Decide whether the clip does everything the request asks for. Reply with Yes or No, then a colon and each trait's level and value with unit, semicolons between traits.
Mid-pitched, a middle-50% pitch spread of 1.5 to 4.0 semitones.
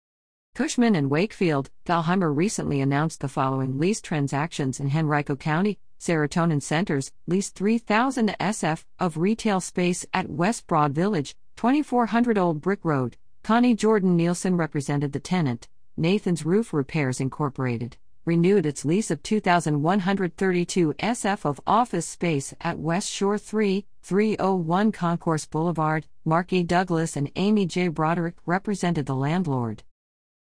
No: medium, 170 Hz; average, 4.9 semitones